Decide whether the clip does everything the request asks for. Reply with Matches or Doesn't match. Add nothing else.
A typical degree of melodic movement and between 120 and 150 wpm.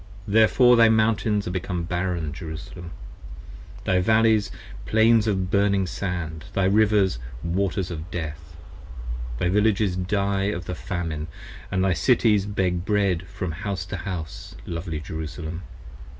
Matches